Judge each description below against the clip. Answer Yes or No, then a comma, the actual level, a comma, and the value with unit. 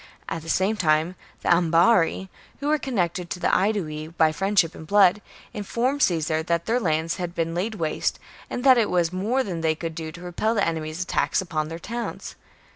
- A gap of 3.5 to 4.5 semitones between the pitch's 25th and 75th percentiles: Yes, average, 4.2 semitones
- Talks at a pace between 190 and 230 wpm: Yes, average, 200 wpm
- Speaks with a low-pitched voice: No, medium, 175 Hz